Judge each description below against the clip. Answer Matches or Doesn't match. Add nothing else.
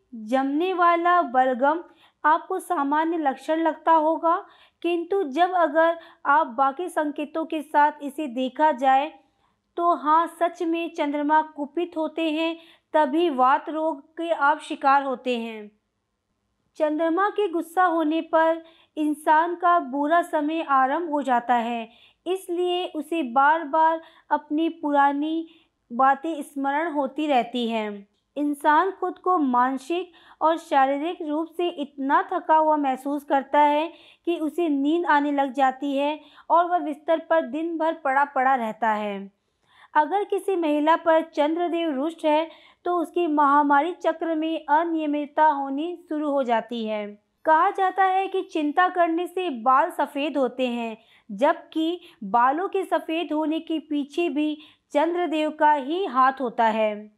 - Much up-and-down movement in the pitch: Doesn't match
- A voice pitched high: Matches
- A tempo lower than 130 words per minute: Doesn't match